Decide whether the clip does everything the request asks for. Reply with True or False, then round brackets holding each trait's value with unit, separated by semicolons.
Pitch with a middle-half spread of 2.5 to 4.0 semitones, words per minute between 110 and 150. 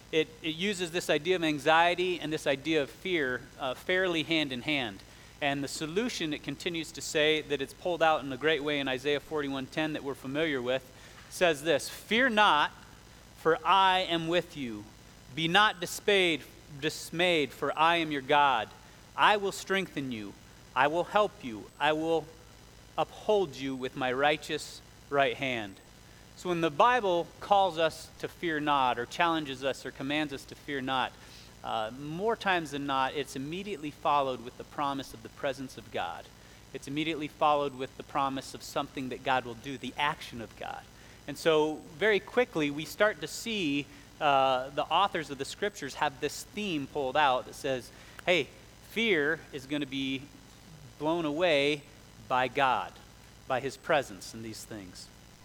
False (3.7 semitones; 175 wpm)